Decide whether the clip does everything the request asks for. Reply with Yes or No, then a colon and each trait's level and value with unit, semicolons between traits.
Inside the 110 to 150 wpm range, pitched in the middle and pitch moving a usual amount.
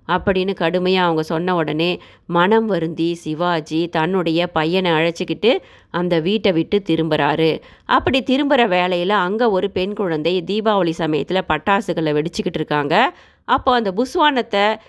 Yes: average, 120 wpm; medium, 180 Hz; average, 3.8 semitones